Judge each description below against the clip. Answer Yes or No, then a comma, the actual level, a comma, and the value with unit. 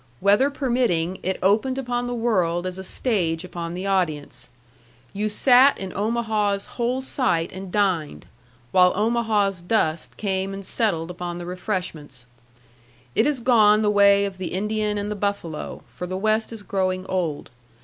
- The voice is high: Yes, high, 200 Hz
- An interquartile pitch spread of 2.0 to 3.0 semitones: No, average, 3.6 semitones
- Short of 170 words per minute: Yes, average, 160 wpm